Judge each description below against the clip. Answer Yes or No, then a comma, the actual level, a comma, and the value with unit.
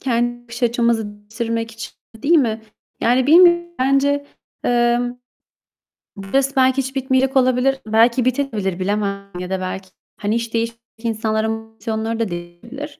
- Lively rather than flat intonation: No, average, 3.2 semitones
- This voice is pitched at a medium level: No, high, 235 Hz